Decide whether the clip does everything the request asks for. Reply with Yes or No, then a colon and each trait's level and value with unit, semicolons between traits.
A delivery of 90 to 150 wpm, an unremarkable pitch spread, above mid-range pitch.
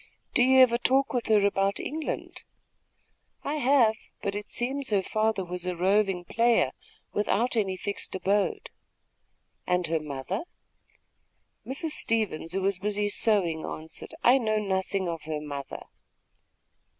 Yes: average, 140 wpm; average, 4.6 semitones; high, 205 Hz